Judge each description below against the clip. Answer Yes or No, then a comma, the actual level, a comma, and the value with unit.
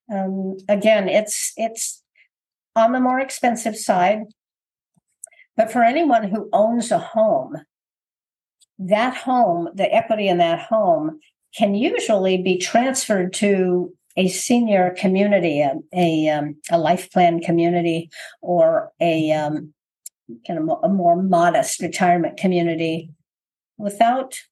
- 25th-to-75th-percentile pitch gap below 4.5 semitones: No, wide, 5.5 semitones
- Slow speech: Yes, slow, 120 wpm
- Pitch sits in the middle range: No, high, 205 Hz